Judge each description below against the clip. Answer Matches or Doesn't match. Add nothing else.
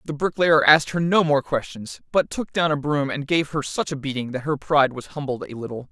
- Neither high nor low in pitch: Matches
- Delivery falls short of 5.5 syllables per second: Doesn't match